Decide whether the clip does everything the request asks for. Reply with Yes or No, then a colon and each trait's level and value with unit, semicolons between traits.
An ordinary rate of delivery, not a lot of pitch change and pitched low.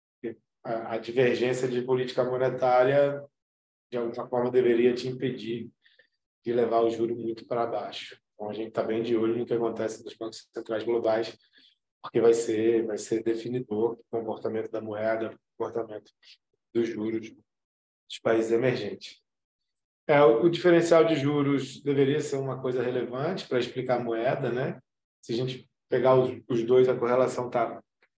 Yes: average, 155 wpm; narrow, 2.1 semitones; low, 120 Hz